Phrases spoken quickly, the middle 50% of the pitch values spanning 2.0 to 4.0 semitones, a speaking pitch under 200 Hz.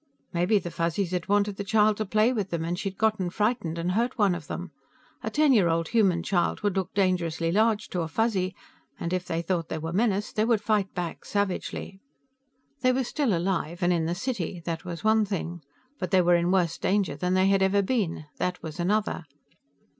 Yes: fast, 215 wpm; average, 3.4 semitones; high, 190 Hz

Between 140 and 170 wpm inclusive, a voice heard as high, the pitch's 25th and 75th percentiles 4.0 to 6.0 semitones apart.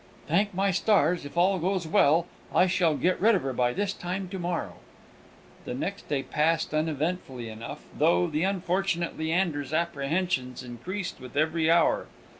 No: average, 160 wpm; medium, 170 Hz; average, 4.4 semitones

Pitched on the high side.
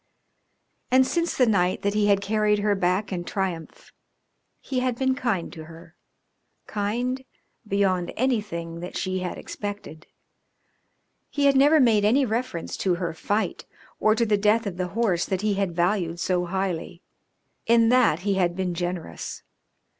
Yes: high, 200 Hz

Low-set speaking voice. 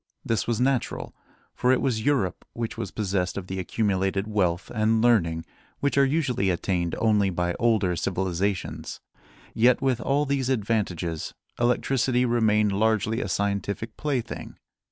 Yes: low, 110 Hz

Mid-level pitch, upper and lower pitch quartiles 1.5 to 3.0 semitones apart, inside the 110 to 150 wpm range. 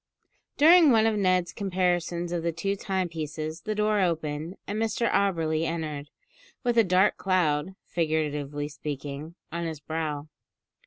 No: medium, 170 Hz; average, 4.0 semitones; average, 140 wpm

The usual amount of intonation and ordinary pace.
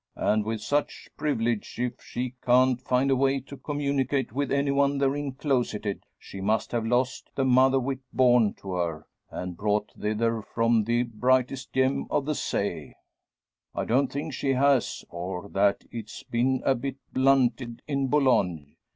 Yes: average, 3.6 semitones; average, 160 wpm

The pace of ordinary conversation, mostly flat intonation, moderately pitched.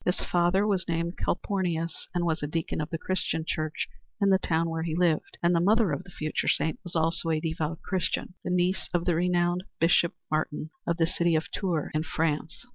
No: fast, 210 wpm; narrow, 1.9 semitones; medium, 170 Hz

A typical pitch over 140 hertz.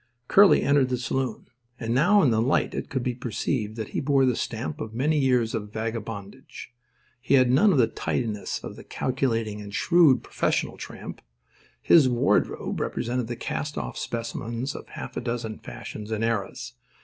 No: low, 120 Hz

